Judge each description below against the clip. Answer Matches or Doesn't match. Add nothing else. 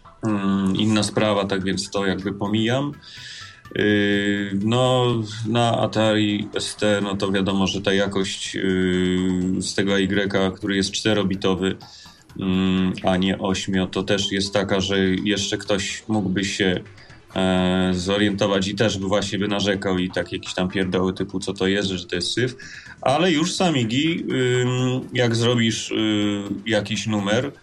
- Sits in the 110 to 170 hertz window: Doesn't match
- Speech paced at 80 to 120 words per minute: Doesn't match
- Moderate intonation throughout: Doesn't match